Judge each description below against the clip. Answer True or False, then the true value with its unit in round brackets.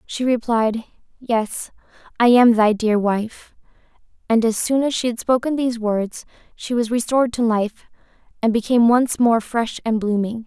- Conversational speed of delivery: True (165 wpm)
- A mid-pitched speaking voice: False (230 Hz)